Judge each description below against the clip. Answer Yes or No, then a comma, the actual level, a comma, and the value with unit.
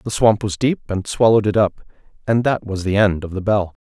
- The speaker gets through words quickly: Yes, fast, 235 wpm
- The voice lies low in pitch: Yes, low, 105 Hz